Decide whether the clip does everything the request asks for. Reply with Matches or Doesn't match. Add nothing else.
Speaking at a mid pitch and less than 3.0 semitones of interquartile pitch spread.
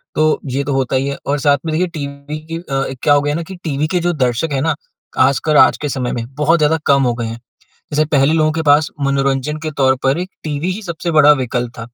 Matches